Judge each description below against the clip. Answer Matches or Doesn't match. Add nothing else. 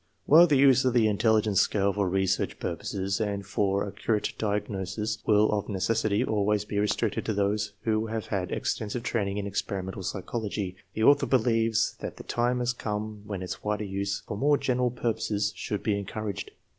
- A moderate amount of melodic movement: Doesn't match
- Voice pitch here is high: Doesn't match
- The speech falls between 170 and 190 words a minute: Matches